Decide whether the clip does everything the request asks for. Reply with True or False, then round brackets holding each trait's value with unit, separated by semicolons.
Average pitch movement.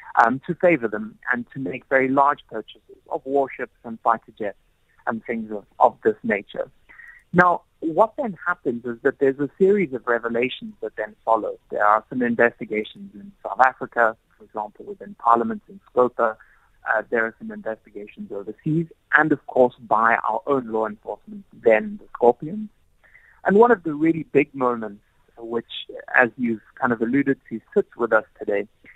False (7.4 semitones)